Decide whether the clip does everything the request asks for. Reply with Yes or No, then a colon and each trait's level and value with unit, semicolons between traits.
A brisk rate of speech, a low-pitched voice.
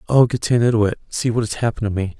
Yes: fast, 220 wpm; low, 115 Hz